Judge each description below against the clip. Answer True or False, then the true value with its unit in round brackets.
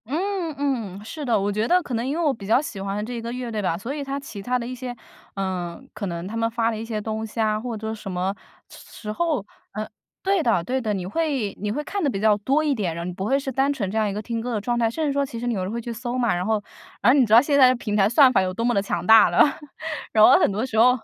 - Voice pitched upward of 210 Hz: True (230 Hz)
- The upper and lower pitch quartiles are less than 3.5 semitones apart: False (4.1 semitones)